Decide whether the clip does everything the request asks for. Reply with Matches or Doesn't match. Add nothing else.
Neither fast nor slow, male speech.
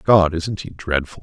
Matches